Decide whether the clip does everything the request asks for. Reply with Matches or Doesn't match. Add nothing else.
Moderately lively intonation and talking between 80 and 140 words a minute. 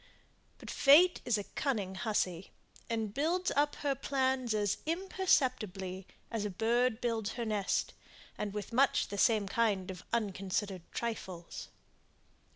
Matches